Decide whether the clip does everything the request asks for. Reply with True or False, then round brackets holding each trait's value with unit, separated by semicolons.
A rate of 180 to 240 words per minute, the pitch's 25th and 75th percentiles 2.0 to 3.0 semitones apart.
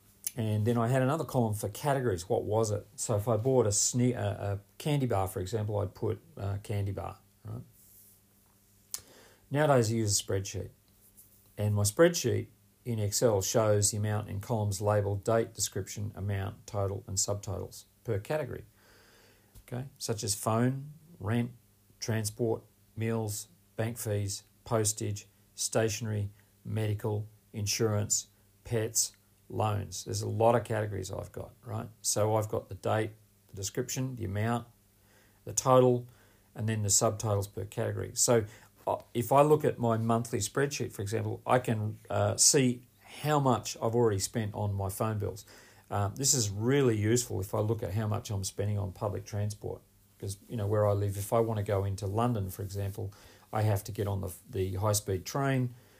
False (165 wpm; 2.7 semitones)